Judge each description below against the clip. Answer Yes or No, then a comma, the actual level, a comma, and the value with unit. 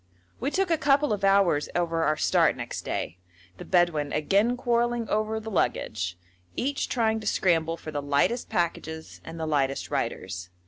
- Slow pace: No, average, 170 wpm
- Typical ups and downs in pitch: No, wide, 7.0 semitones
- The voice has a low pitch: No, medium, 175 Hz